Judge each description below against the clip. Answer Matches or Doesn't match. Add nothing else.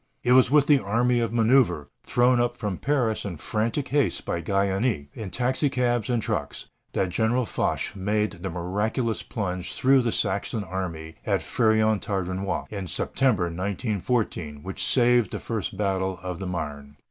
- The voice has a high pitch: Doesn't match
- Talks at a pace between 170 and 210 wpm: Doesn't match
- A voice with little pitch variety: Doesn't match